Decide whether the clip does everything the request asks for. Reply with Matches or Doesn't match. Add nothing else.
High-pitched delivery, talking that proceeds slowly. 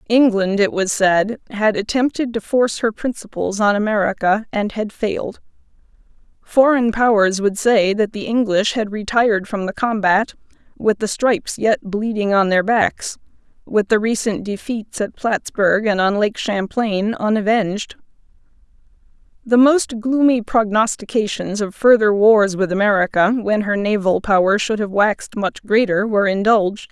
Doesn't match